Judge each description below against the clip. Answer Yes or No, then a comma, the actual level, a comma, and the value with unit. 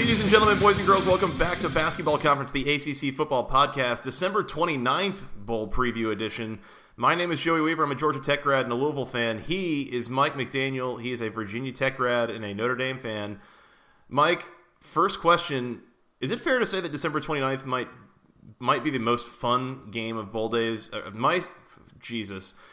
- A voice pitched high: No, low, 135 Hz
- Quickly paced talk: No, average, 195 wpm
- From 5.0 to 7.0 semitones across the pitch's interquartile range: Yes, wide, 5.5 semitones